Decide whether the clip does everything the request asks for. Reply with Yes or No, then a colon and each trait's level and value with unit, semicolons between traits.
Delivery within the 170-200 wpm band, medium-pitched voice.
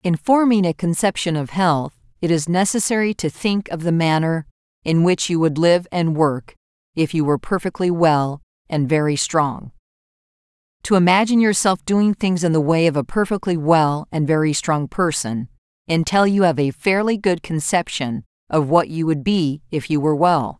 Yes: average, 180 wpm; medium, 165 Hz